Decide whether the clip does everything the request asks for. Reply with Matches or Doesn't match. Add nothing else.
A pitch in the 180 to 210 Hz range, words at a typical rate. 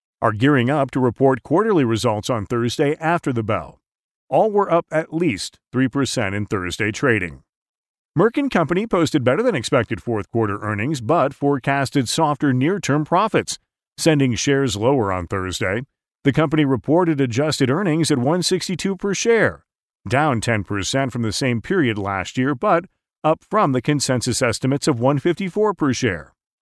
Doesn't match